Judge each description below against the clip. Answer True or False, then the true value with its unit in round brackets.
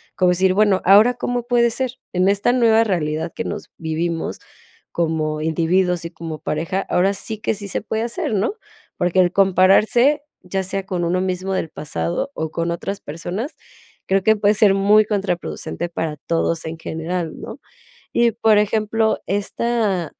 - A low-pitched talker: False (190 Hz)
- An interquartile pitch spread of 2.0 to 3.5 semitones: False (4.1 semitones)